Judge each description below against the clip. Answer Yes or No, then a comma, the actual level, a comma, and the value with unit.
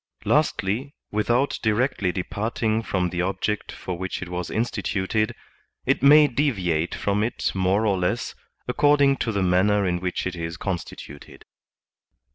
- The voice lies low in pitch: Yes, low, 100 Hz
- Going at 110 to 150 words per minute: Yes, average, 140 wpm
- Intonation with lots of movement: No, average, 4.3 semitones